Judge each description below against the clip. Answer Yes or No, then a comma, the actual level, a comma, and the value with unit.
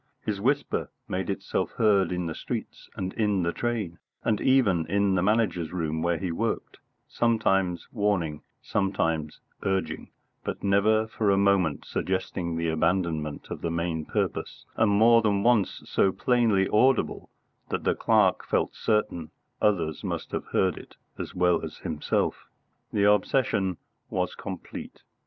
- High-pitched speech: No, very low, 95 Hz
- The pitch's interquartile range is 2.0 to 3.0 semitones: No, average, 3.8 semitones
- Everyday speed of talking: Yes, average, 145 wpm